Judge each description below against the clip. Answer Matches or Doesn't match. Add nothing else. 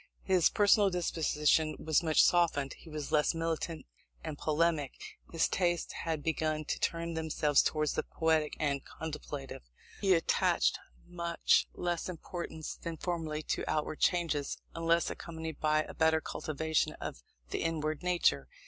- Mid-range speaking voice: Matches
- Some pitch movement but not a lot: Doesn't match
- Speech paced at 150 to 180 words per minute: Doesn't match